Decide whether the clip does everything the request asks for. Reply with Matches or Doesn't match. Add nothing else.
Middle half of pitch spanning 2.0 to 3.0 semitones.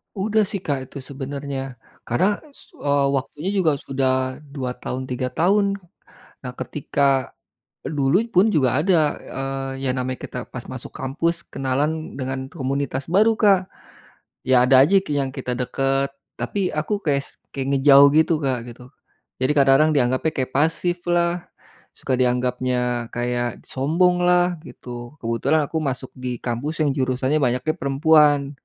Doesn't match